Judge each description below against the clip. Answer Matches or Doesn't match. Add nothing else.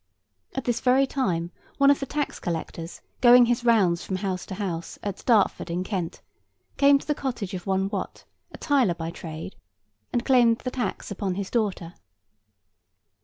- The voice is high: Matches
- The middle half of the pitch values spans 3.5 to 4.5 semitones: Doesn't match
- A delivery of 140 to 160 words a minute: Doesn't match